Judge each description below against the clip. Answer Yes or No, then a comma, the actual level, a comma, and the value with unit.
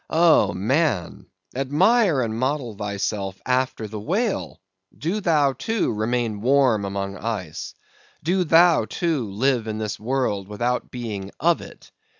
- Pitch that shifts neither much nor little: No, wide, 6.5 semitones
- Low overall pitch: Yes, low, 125 Hz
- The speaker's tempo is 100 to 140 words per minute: Yes, slow, 135 wpm